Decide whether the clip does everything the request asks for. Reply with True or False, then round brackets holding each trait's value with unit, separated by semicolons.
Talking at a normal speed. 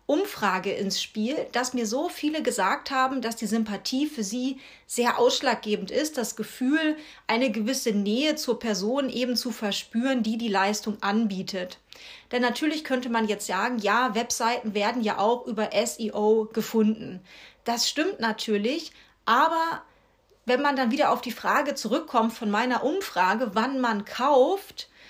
True (150 wpm)